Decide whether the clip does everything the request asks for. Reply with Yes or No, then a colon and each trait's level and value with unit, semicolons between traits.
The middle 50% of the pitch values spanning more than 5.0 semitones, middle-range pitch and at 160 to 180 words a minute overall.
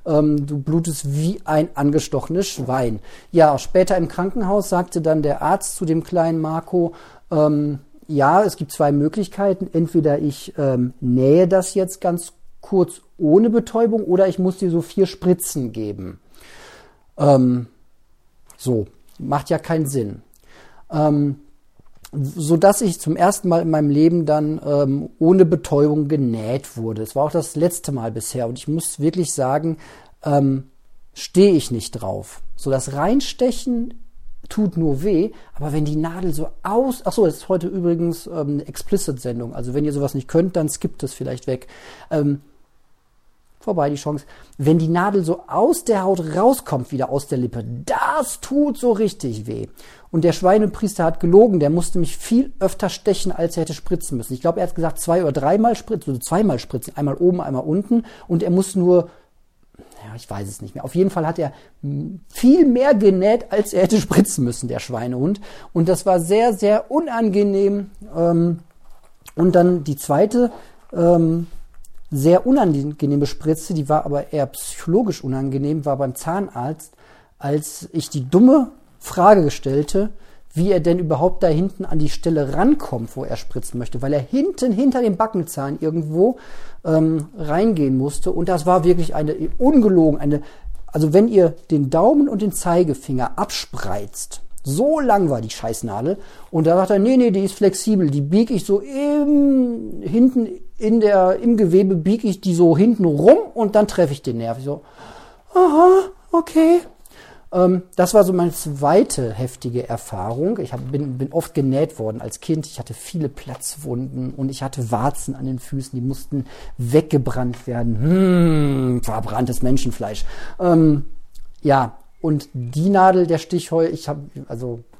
Yes: wide, 5.4 semitones; medium, 165 Hz; average, 165 wpm